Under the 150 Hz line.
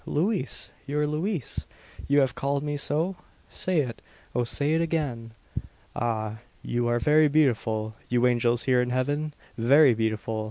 Yes: low, 135 Hz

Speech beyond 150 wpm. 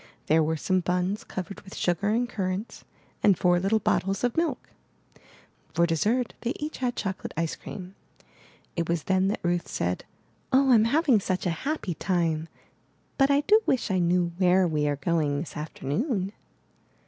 Yes: average, 170 wpm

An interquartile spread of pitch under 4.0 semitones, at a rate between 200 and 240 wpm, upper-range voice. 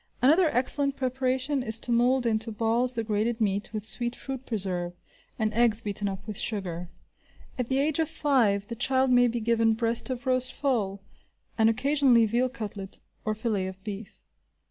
No: average, 3.3 semitones; average, 175 wpm; high, 230 Hz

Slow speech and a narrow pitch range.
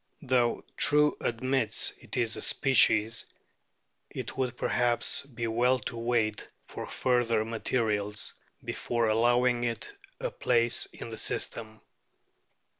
Yes: slow, 115 wpm; narrow, 1.9 semitones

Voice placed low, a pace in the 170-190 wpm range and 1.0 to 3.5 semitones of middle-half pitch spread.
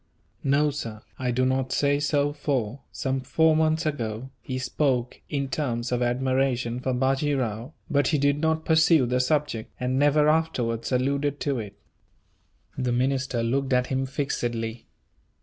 No: low, 130 Hz; average, 155 wpm; average, 2.8 semitones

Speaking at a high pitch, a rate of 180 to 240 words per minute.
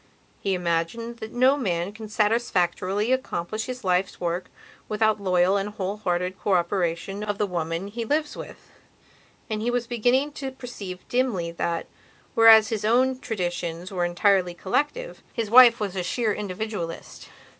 No: high, 205 Hz; average, 150 wpm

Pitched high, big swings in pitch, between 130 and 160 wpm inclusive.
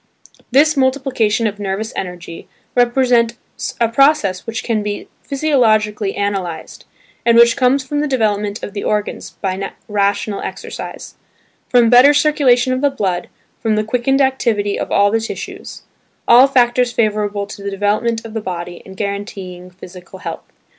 No: high, 220 Hz; average, 3.8 semitones; average, 145 wpm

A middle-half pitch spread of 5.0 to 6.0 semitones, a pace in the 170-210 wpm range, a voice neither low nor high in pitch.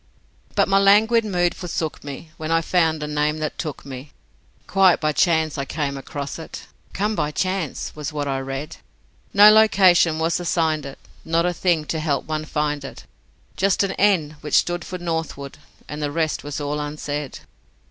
No: average, 3.1 semitones; average, 180 wpm; medium, 155 Hz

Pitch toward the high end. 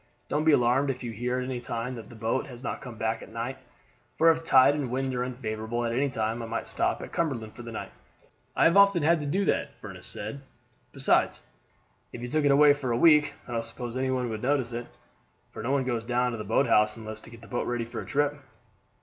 No: low, 125 Hz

